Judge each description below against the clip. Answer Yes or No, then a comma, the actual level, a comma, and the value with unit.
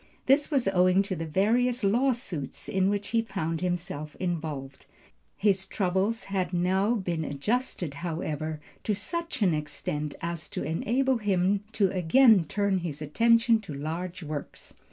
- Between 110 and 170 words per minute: Yes, average, 145 wpm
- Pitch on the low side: No, medium, 185 Hz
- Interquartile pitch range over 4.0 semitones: Yes, average, 5.2 semitones